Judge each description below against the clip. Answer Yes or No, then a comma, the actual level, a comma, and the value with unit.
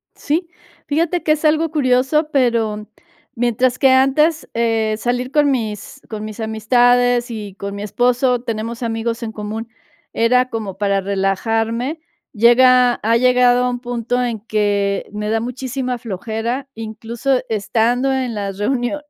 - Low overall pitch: No, high, 235 Hz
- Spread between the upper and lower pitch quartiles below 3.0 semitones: Yes, narrow, 2.6 semitones